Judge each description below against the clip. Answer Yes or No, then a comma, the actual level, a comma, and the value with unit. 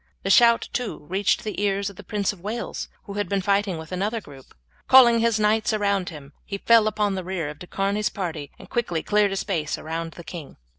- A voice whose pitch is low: No, high, 200 Hz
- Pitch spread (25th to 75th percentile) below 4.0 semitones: Yes, average, 3.3 semitones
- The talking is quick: Yes, fast, 225 wpm